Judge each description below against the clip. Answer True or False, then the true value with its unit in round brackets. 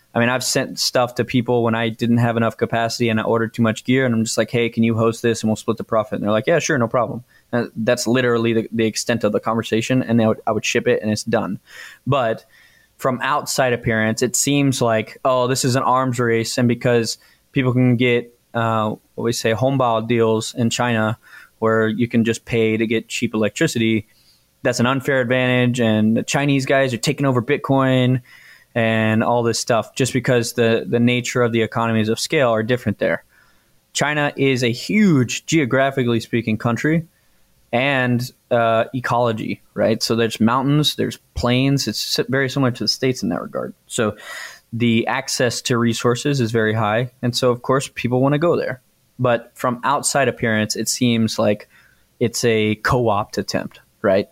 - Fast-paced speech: False (195 wpm)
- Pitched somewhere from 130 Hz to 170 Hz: False (120 Hz)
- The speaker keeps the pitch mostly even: True (2.2 semitones)